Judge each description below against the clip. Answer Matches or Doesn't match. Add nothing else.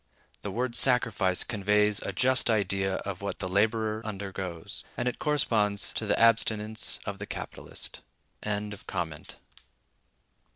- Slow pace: Matches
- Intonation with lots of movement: Doesn't match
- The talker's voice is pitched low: Matches